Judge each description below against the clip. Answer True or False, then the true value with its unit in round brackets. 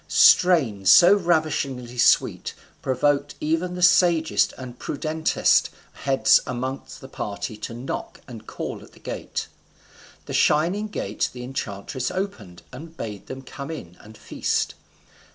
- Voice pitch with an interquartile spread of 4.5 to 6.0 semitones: True (5.5 semitones)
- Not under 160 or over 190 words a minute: False (135 wpm)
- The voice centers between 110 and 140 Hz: True (135 Hz)